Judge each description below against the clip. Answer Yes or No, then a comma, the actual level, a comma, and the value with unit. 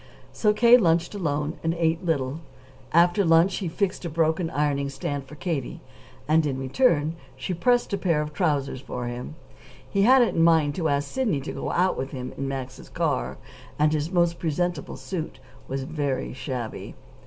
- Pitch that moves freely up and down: No, average, 3.9 semitones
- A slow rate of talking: No, average, 180 wpm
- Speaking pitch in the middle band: Yes, medium, 160 Hz